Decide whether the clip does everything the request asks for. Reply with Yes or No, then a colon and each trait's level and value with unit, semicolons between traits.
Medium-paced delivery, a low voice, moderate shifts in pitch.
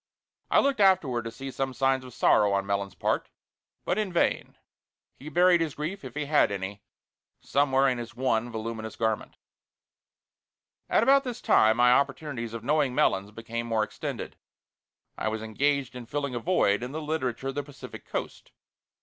Yes: average, 175 wpm; low, 130 Hz; average, 4.7 semitones